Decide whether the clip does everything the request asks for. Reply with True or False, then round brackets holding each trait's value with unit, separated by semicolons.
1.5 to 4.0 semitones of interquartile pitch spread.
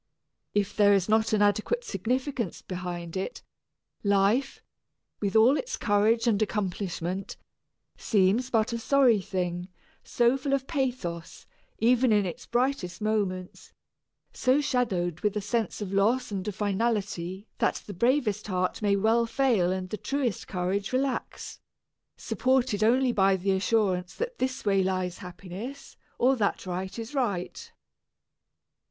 False (4.7 semitones)